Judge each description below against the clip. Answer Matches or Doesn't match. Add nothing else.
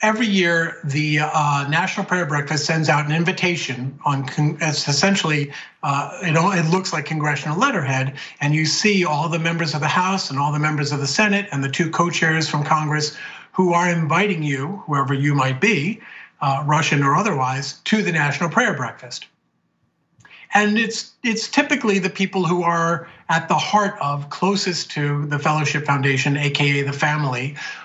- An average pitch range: Matches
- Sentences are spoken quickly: Doesn't match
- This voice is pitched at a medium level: Matches